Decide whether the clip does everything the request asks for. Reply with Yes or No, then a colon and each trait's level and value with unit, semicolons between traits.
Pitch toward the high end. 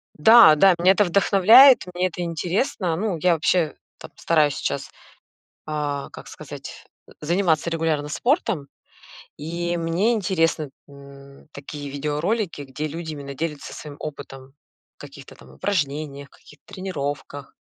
No: medium, 160 Hz